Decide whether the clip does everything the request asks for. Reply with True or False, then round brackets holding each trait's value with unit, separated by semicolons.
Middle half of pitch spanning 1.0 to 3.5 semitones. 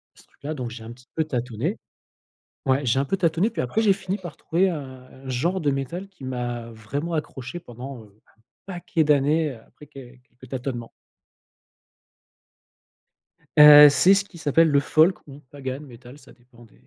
False (4.7 semitones)